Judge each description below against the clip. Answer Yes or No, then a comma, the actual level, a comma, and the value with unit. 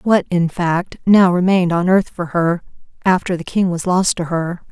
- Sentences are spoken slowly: No, fast, 205 wpm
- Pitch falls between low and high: Yes, medium, 180 Hz